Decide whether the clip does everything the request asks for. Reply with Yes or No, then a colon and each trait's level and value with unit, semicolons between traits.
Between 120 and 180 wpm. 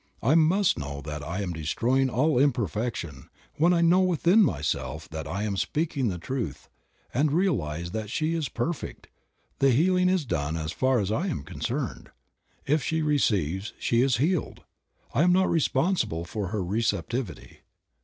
Yes: average, 165 wpm